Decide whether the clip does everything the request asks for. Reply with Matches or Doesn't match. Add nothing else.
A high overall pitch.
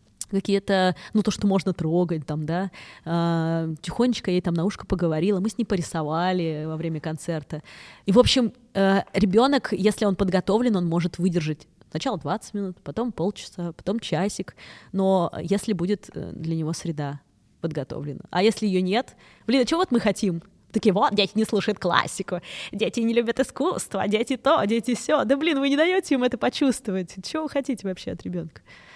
Matches